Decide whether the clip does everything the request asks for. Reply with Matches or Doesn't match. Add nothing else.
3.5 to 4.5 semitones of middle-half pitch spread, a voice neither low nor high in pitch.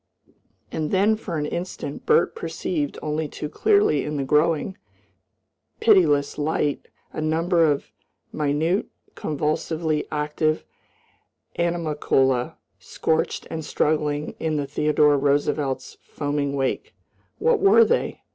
Doesn't match